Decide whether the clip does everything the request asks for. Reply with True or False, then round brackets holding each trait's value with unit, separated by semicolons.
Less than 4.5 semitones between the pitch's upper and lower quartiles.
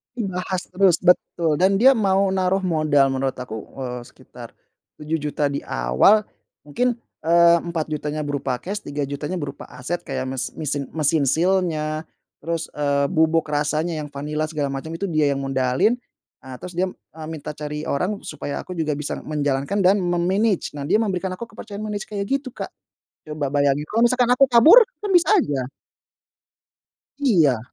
False (4.9 semitones)